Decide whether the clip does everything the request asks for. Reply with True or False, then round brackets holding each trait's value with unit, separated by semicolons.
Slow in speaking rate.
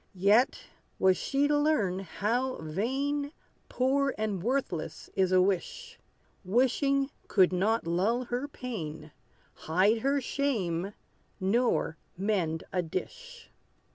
True (110 wpm)